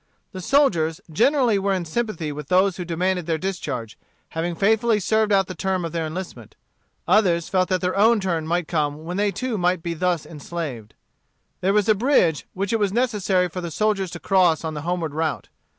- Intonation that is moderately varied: Yes, average, 3.6 semitones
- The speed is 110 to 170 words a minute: No, average, 200 wpm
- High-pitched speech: No, medium, 180 Hz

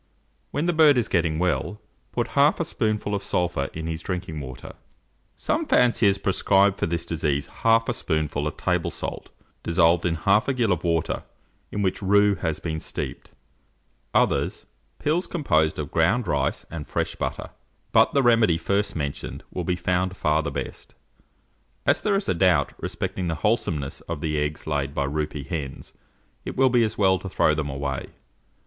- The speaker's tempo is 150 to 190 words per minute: Yes, average, 180 wpm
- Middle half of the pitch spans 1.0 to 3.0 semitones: No, average, 4.8 semitones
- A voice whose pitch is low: Yes, very low, 85 Hz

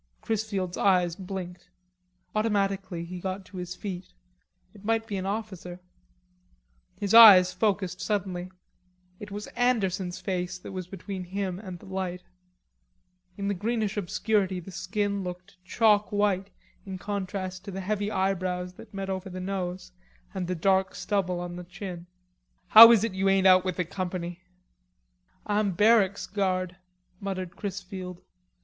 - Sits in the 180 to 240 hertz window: Yes, high, 190 Hz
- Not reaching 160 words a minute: Yes, average, 145 wpm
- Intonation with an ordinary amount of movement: No, narrow, 1.9 semitones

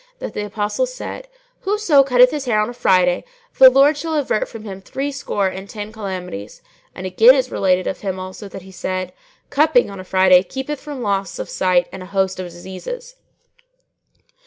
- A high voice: Yes, high, 205 Hz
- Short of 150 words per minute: No, average, 185 wpm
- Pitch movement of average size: No, wide, 6.5 semitones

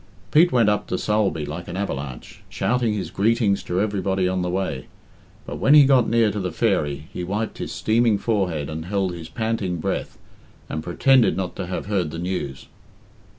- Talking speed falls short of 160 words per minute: No, average, 190 wpm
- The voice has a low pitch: Yes, very low, 95 Hz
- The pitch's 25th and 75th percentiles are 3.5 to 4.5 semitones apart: Yes, average, 4.2 semitones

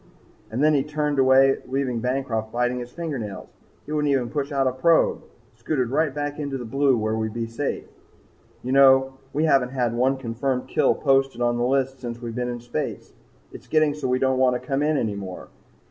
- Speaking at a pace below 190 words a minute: No, fast, 205 wpm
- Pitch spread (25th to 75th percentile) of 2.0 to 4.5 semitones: Yes, narrow, 2.5 semitones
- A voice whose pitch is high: No, low, 130 Hz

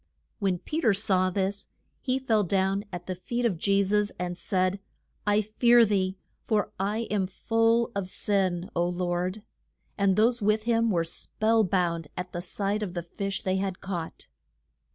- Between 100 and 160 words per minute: No, average, 170 wpm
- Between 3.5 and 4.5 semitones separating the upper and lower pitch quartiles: No, average, 2.8 semitones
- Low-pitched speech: No, high, 195 Hz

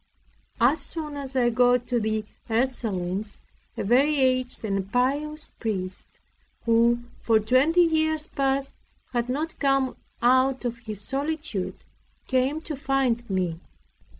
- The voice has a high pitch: Yes, very high, 255 Hz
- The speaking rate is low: Yes, slow, 125 wpm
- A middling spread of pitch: Yes, average, 3.5 semitones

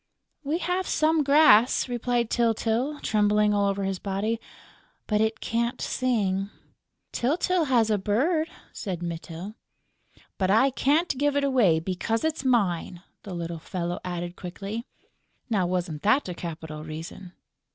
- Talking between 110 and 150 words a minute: Yes, average, 140 wpm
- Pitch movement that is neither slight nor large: No, wide, 6.0 semitones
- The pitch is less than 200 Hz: No, high, 210 Hz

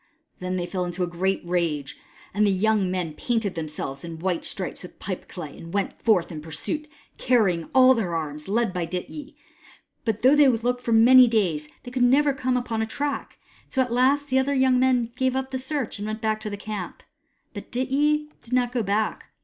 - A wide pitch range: Yes, wide, 6.2 semitones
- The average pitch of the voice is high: Yes, high, 220 Hz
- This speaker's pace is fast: Yes, fast, 215 wpm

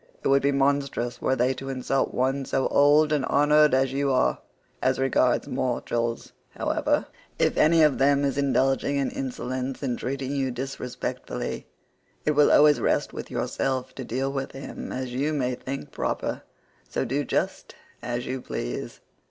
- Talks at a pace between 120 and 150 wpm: No, average, 165 wpm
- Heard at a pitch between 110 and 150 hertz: Yes, low, 135 Hz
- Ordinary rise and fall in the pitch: No, narrow, 1.7 semitones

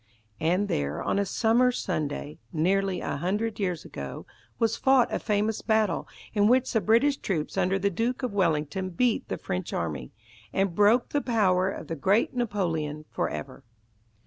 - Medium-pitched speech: No, high, 195 Hz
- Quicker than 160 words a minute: Yes, average, 170 wpm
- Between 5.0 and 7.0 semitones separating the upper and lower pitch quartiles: Yes, average, 5.3 semitones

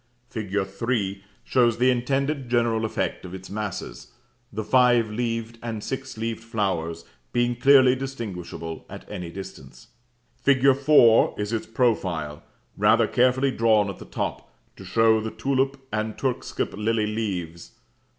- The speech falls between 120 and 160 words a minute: Yes, average, 140 wpm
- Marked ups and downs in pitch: No, average, 3.7 semitones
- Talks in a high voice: No, low, 115 Hz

